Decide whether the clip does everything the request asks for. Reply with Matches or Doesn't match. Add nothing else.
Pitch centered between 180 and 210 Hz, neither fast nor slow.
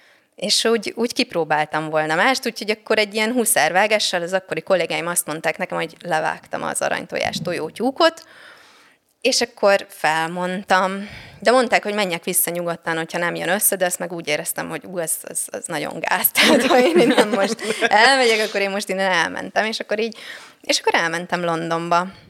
Doesn't match